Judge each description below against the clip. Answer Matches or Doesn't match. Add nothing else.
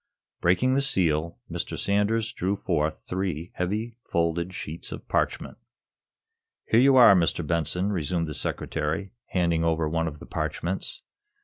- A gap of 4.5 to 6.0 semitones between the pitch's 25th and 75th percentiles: Doesn't match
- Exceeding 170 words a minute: Doesn't match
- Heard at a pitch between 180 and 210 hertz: Doesn't match